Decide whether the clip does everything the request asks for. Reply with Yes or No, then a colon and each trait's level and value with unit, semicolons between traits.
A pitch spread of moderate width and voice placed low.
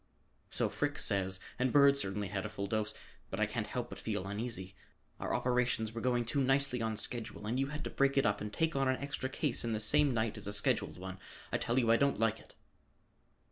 Yes: average, 4.4 semitones; low, 115 Hz